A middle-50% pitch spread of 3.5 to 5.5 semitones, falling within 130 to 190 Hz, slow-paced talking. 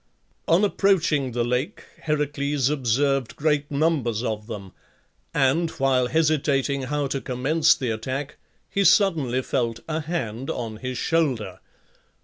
Yes: average, 3.8 semitones; low, 135 Hz; slow, 125 wpm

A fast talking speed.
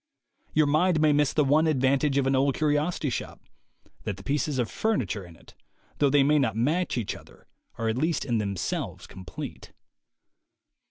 No: average, 180 wpm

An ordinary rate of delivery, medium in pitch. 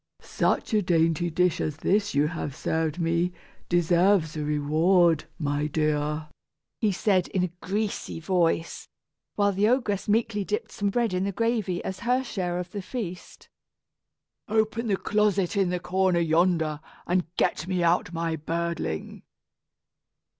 Yes: average, 145 wpm; medium, 180 Hz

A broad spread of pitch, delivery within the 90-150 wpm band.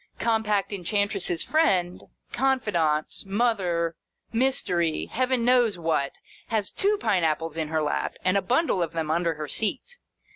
Yes: wide, 6.1 semitones; average, 140 wpm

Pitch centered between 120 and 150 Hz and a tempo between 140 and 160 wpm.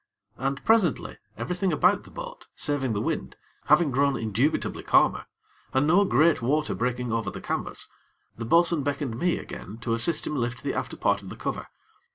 No: medium, 140 Hz; average, 180 wpm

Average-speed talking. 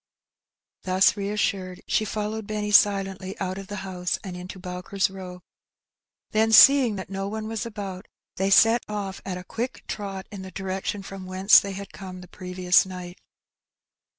Yes: average, 165 wpm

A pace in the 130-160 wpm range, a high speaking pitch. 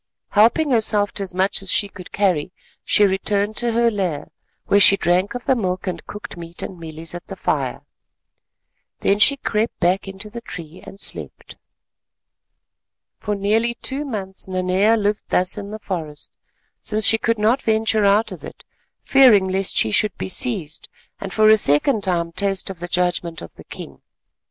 No: average, 175 wpm; high, 200 Hz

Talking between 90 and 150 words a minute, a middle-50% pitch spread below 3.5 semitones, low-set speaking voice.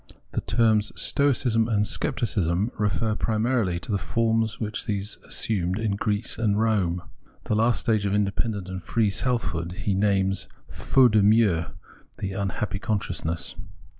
Yes: average, 145 wpm; narrow, 2.6 semitones; low, 105 Hz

